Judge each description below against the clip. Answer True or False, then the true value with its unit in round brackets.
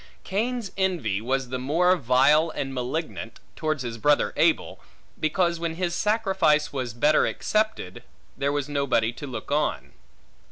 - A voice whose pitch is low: False (150 Hz)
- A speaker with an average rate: True (150 wpm)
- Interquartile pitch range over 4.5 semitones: True (5.3 semitones)